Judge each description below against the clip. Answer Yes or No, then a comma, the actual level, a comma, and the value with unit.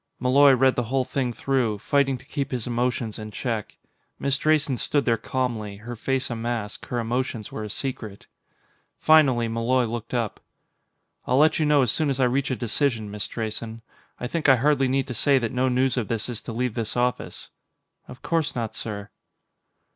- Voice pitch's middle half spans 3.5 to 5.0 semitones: No, average, 2.8 semitones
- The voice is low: Yes, low, 125 Hz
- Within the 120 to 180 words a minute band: No, average, 190 wpm